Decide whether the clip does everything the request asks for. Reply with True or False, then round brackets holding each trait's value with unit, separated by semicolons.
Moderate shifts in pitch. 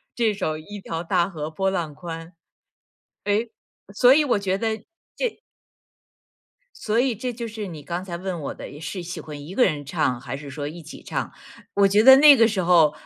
False (5.7 semitones)